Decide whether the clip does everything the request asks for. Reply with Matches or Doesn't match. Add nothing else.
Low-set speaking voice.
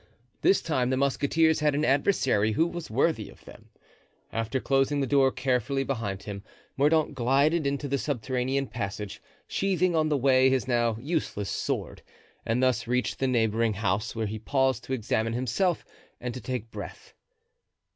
Matches